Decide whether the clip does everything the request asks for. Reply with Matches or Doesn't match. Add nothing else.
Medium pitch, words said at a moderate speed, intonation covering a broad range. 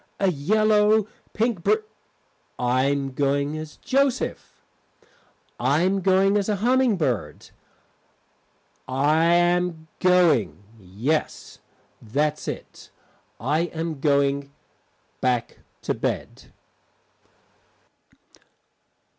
Doesn't match